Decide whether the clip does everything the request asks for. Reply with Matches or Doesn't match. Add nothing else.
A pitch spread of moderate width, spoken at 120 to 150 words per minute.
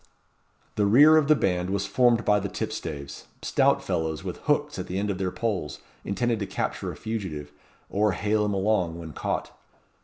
Doesn't match